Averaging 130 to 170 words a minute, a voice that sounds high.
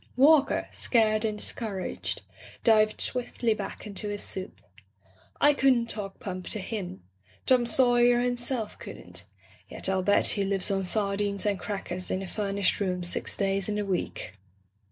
Yes: average, 155 wpm; high, 205 Hz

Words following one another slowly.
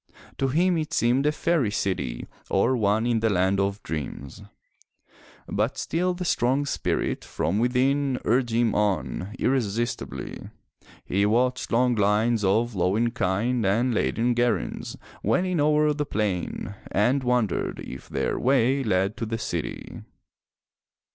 No: average, 150 wpm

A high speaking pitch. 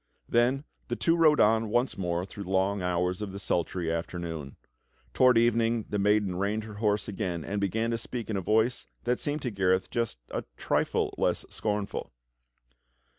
No: low, 105 Hz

